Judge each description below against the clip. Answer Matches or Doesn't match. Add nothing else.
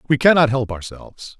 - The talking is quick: Doesn't match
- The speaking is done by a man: Matches